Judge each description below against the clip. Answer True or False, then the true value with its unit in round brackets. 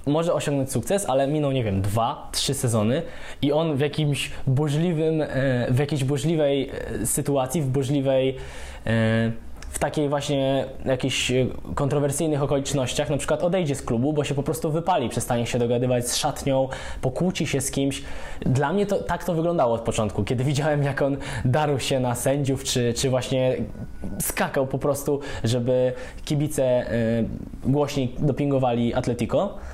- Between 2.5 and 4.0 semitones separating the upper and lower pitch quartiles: True (2.9 semitones)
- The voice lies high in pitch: False (135 Hz)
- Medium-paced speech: True (145 wpm)